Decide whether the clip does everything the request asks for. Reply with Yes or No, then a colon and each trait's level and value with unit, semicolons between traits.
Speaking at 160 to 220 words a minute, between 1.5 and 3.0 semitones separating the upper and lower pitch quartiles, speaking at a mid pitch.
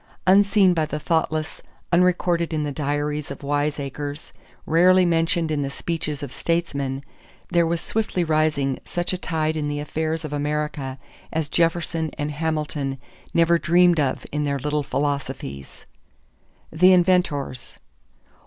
No: slow, 135 wpm; average, 2.7 semitones; medium, 155 Hz